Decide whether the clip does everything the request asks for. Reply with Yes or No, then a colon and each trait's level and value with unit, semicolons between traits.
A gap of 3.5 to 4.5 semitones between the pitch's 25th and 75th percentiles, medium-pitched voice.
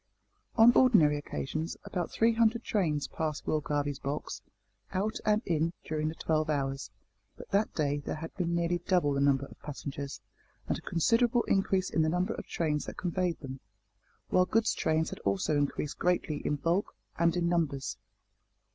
Yes: average, 4.0 semitones; medium, 160 Hz